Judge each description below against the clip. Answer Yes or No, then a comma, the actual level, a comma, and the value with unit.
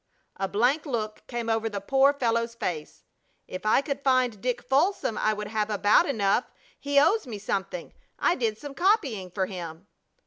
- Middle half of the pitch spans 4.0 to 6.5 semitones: Yes, average, 4.9 semitones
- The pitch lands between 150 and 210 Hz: No, high, 230 Hz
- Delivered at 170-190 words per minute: Yes, average, 175 wpm